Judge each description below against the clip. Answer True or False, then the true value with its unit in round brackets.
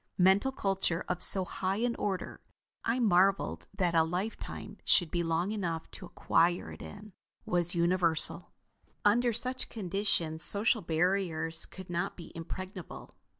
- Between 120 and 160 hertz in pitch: False (185 Hz)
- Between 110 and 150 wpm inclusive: True (140 wpm)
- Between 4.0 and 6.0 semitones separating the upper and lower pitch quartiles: False (3.1 semitones)